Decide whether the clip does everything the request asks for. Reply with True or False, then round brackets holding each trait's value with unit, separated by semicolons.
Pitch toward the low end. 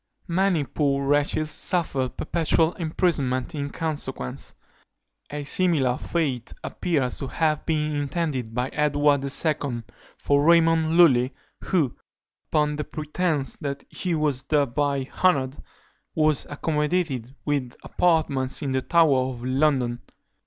False (145 Hz)